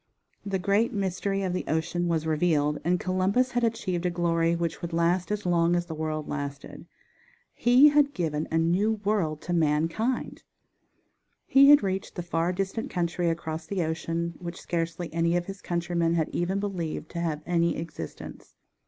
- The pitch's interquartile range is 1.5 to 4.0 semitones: Yes, average, 2.7 semitones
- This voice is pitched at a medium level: Yes, medium, 175 Hz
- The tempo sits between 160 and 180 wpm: Yes, average, 170 wpm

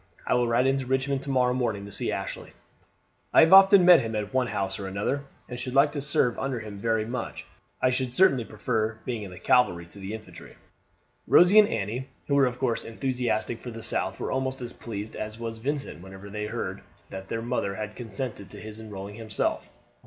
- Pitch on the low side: Yes, low, 115 Hz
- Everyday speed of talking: No, fast, 210 wpm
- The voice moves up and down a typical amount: Yes, average, 3.7 semitones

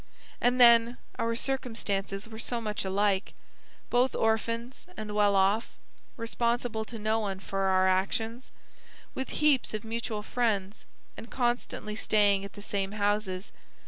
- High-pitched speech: Yes, high, 220 Hz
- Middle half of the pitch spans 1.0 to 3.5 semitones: Yes, average, 2.7 semitones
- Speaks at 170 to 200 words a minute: No, average, 140 wpm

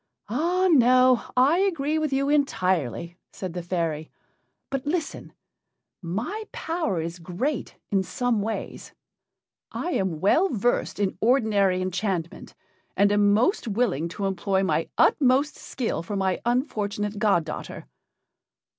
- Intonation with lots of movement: Yes, wide, 6.5 semitones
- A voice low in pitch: No, high, 210 Hz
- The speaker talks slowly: Yes, slow, 130 wpm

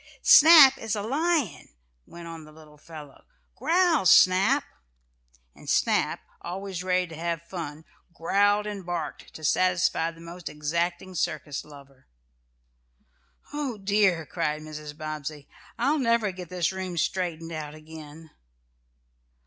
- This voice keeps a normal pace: No, slow, 125 wpm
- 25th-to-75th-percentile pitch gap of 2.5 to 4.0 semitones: No, average, 4.5 semitones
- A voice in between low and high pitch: Yes, medium, 170 Hz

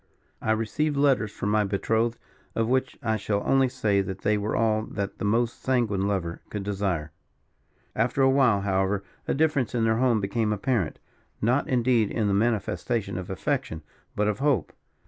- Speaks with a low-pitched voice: Yes, low, 110 Hz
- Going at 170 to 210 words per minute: Yes, average, 175 wpm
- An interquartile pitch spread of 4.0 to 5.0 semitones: No, average, 3.6 semitones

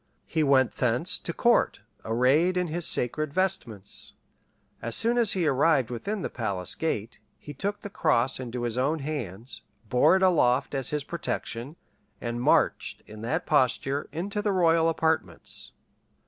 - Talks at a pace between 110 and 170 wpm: Yes, average, 155 wpm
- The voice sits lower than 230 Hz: Yes, medium, 140 Hz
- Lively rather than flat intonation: Yes, wide, 5.7 semitones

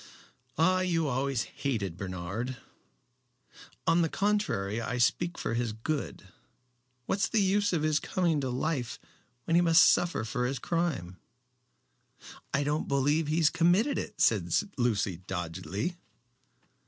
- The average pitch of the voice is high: No, medium, 140 Hz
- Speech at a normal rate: No, slow, 130 wpm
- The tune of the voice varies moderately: No, wide, 7.1 semitones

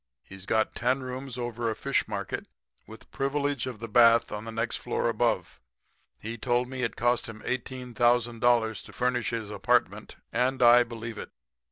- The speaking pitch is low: Yes, low, 120 Hz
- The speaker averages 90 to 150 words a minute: No, average, 170 wpm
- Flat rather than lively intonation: Yes, narrow, 2.0 semitones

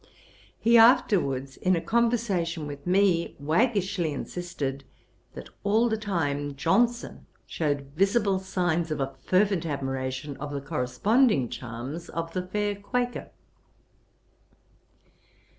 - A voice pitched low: No, medium, 170 Hz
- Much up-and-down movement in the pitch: Yes, wide, 6.4 semitones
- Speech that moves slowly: Yes, slow, 110 wpm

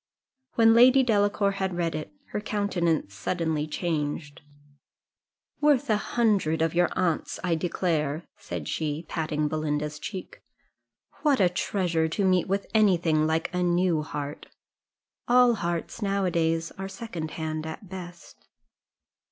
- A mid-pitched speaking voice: Yes, medium, 175 Hz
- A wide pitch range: No, average, 4.1 semitones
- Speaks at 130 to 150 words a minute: Yes, average, 140 wpm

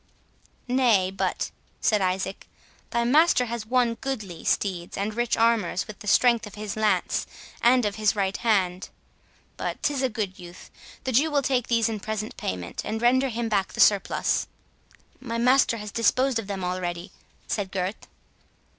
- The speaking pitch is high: Yes, high, 215 Hz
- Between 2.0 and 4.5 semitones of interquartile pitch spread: Yes, average, 3.8 semitones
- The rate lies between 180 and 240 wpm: No, average, 160 wpm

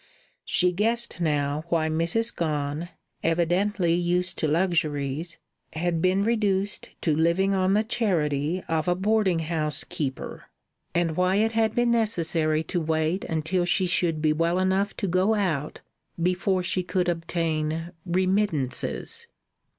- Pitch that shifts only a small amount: No, average, 3.3 semitones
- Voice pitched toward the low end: No, medium, 175 Hz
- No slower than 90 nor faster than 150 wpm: Yes, slow, 135 wpm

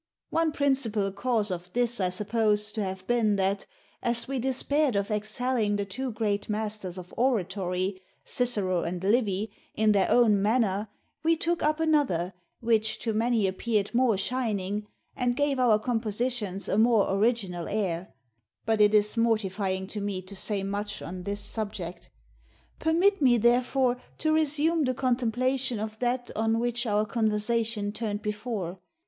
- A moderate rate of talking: Yes, average, 155 wpm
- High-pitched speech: Yes, high, 220 Hz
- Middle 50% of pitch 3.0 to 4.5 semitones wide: Yes, average, 3.6 semitones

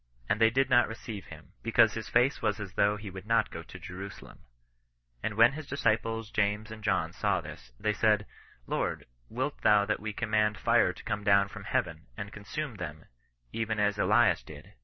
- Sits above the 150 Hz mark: No, low, 105 Hz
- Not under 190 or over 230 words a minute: Yes, average, 195 wpm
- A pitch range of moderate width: No, narrow, 1.8 semitones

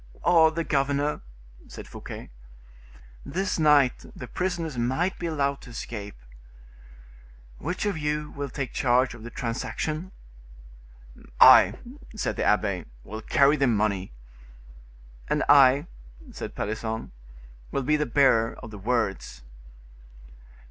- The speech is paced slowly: Yes, slow, 120 wpm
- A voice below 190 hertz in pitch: Yes, low, 135 Hz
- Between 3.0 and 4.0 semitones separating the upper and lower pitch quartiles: No, average, 4.8 semitones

